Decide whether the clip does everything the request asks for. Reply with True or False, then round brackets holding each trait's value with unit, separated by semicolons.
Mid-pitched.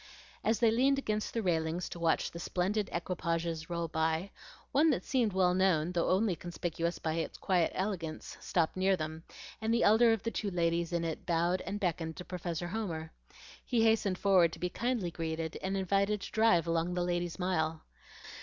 True (180 Hz)